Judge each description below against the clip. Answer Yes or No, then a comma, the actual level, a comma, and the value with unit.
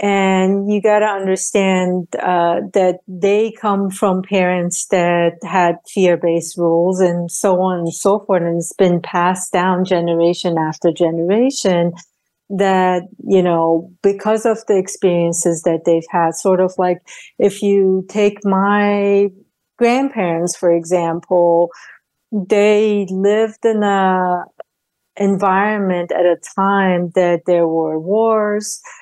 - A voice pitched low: No, medium, 185 Hz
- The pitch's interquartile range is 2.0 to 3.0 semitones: Yes, narrow, 2.6 semitones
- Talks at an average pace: No, slow, 125 wpm